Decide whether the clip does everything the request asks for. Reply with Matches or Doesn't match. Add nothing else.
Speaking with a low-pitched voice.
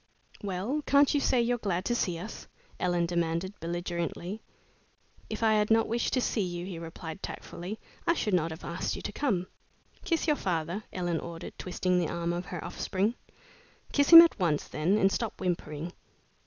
Doesn't match